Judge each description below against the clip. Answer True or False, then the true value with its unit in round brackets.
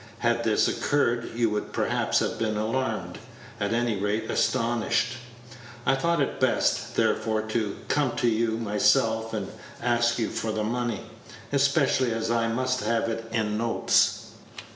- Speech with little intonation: True (1.6 semitones)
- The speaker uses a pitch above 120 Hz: False (115 Hz)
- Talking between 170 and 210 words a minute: False (150 wpm)